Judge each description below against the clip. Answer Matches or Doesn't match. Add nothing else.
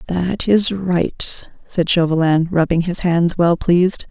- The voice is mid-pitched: Matches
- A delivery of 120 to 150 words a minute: Matches